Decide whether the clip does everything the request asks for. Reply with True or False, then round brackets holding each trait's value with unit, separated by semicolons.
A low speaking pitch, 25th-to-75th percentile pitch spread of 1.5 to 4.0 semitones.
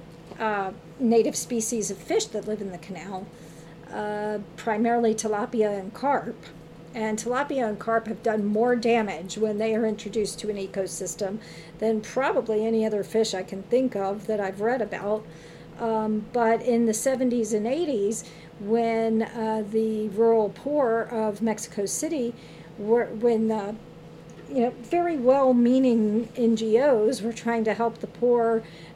False (220 Hz; 2.4 semitones)